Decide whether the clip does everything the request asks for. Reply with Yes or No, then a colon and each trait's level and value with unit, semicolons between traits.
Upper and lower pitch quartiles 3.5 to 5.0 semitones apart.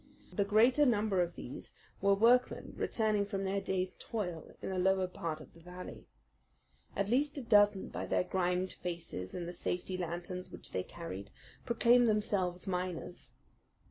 No: average, 3.1 semitones